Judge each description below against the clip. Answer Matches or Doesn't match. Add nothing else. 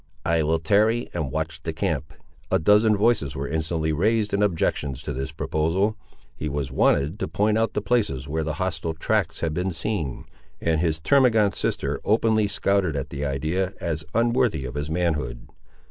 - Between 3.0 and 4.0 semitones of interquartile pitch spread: Doesn't match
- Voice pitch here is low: Matches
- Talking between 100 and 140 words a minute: Doesn't match